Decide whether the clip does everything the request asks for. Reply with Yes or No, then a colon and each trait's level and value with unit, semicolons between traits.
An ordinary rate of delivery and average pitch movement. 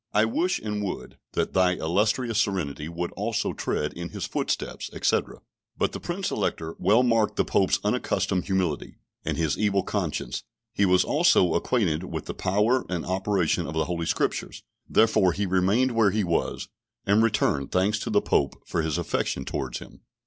Yes: average, 175 wpm; average, 4.1 semitones